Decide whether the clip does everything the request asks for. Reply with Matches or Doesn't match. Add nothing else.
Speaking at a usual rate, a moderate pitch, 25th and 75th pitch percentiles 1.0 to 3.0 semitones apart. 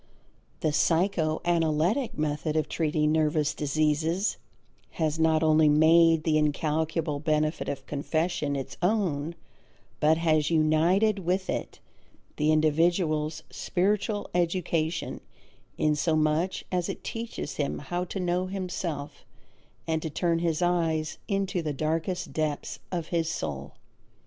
Doesn't match